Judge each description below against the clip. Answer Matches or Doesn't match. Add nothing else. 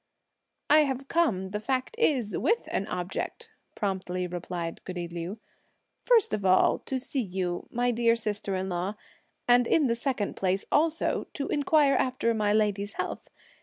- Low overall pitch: Doesn't match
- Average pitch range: Doesn't match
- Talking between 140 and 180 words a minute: Matches